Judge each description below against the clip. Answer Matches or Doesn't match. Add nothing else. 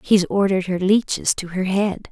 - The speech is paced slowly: Doesn't match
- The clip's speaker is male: Doesn't match